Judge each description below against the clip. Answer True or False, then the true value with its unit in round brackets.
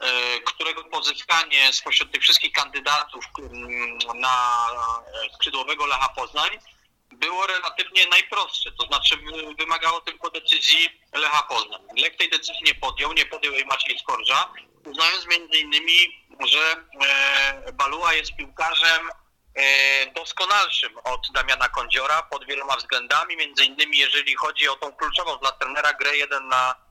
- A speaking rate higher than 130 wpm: False (125 wpm)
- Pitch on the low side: False (150 Hz)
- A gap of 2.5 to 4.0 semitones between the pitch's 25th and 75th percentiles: True (3.5 semitones)